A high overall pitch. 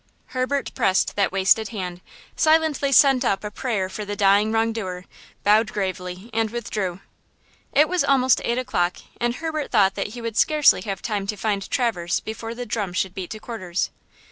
Yes: high, 215 Hz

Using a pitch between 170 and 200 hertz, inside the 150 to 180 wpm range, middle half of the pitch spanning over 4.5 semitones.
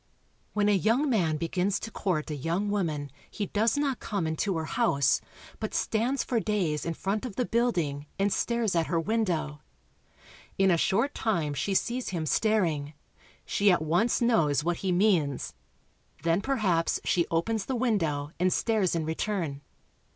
Yes: high, 190 Hz; average, 165 wpm; wide, 5.4 semitones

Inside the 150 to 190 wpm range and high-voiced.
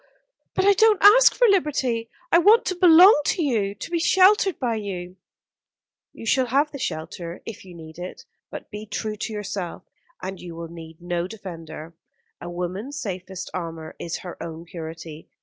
Yes: average, 175 wpm; high, 200 Hz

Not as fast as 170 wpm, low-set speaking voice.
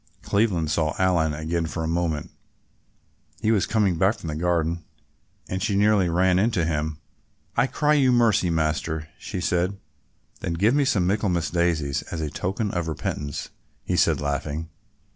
Yes: average, 160 wpm; very low, 85 Hz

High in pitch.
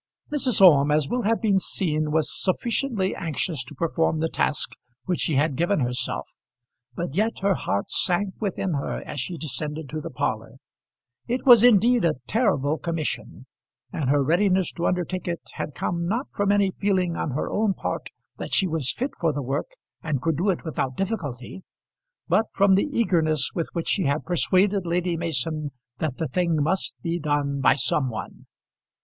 No: medium, 170 Hz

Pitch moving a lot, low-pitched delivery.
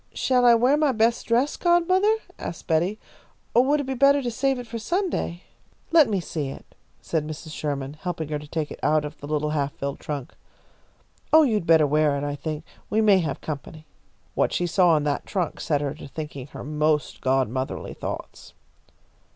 No: wide, 8.5 semitones; medium, 160 Hz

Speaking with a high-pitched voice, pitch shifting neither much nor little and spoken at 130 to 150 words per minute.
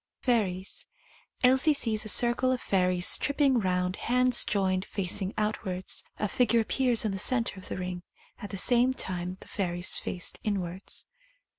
No: high, 205 Hz; average, 4.8 semitones; average, 160 wpm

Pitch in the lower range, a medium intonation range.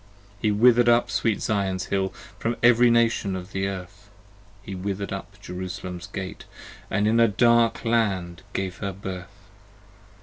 Yes: low, 100 Hz; average, 3.5 semitones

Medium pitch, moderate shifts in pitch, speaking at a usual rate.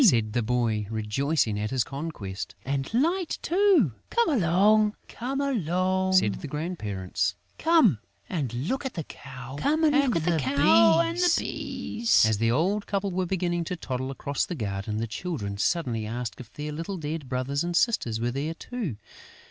No: medium, 150 Hz; wide, 8.6 semitones; average, 150 wpm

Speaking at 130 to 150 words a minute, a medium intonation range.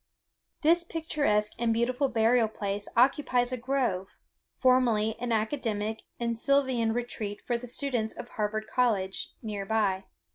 Yes: slow, 135 wpm; average, 3.1 semitones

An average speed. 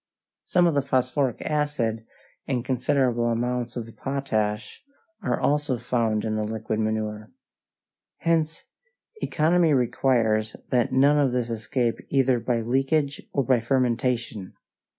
No: slow, 130 wpm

